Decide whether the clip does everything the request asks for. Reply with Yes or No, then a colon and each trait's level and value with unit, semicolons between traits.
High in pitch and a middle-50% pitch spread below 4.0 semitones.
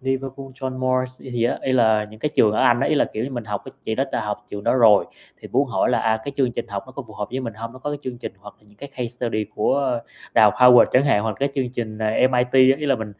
No: low, 120 Hz; average, 3.3 semitones